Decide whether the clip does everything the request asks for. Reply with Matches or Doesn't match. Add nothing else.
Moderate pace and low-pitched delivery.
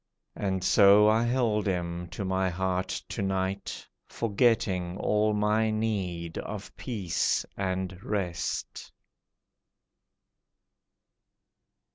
Doesn't match